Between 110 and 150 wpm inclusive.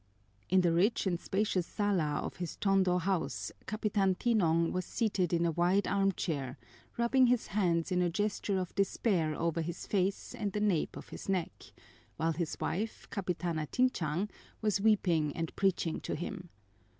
No: average, 160 wpm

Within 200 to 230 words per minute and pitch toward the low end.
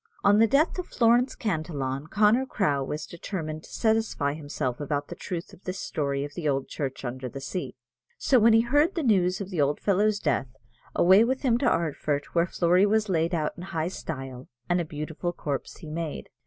No: fast, 205 wpm; medium, 170 Hz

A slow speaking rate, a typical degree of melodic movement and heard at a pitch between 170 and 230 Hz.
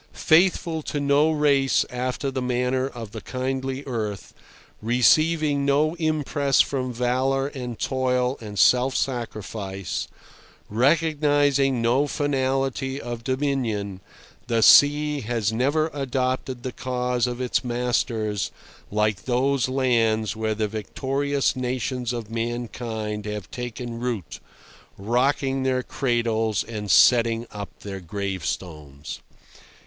No: slow, 110 wpm; average, 3.4 semitones; low, 125 Hz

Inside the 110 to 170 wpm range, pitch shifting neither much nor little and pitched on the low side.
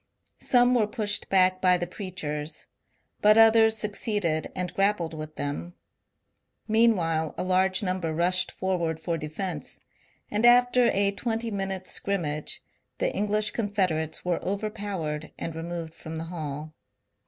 No: slow, 135 wpm; average, 4.4 semitones; medium, 185 Hz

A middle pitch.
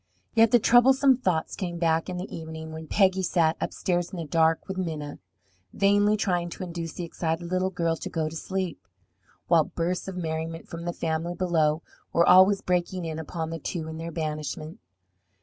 Yes: medium, 170 Hz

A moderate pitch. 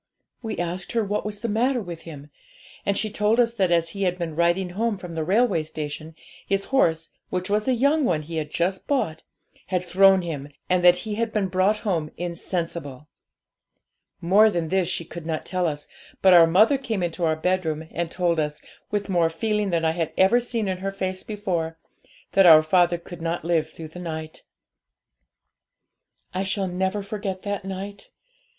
Yes: medium, 180 Hz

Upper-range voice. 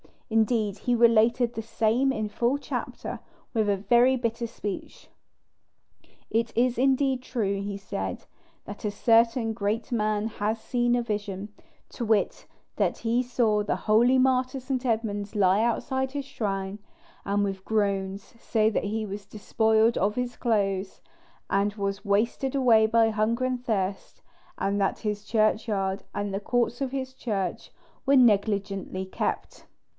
Yes: high, 220 Hz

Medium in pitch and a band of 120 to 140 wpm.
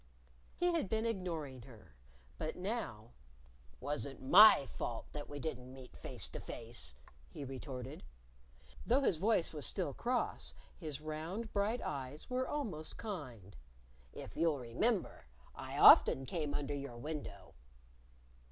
Yes: medium, 150 Hz; slow, 135 wpm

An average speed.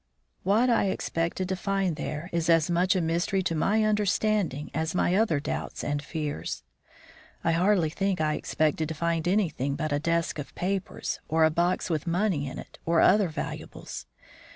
Yes: average, 175 wpm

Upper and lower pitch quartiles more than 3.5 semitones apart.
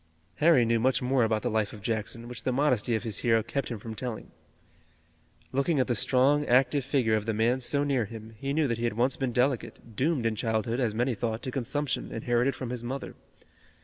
No: average, 2.9 semitones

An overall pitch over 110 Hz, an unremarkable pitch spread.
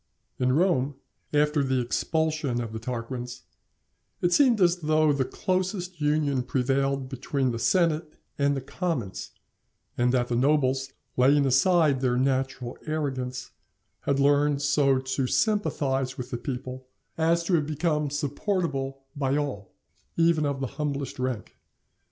Yes: medium, 140 Hz; average, 3.1 semitones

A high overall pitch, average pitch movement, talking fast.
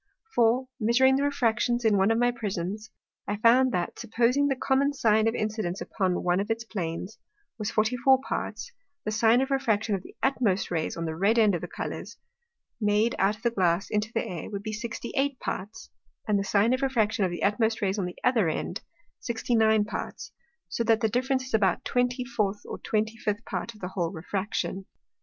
Yes: high, 220 Hz; average, 3.2 semitones; fast, 210 wpm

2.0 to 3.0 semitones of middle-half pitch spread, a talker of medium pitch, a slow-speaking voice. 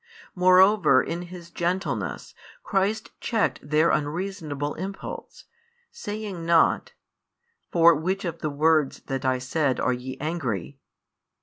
No: average, 4.4 semitones; medium, 170 Hz; slow, 115 wpm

